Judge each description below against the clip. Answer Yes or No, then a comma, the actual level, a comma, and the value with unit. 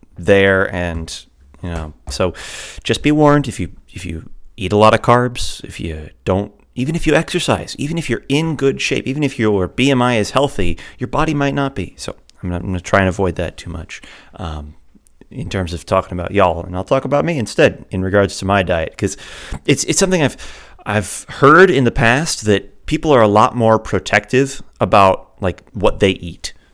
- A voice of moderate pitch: No, low, 105 Hz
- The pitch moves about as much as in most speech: No, wide, 7.1 semitones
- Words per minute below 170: No, fast, 205 wpm